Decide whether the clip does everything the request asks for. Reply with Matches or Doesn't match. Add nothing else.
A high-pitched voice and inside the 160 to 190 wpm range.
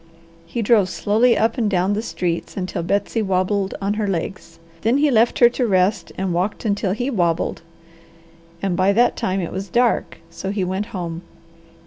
Matches